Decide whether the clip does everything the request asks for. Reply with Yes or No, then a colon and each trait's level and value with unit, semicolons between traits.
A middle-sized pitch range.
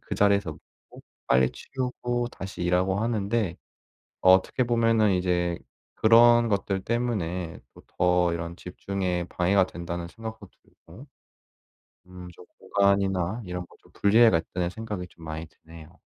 Yes: average, 4.1 semitones